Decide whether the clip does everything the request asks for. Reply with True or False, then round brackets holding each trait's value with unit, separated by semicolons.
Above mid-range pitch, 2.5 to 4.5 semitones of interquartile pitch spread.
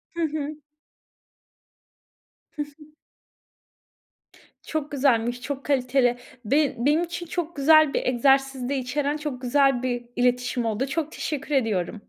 True (275 Hz; 3.2 semitones)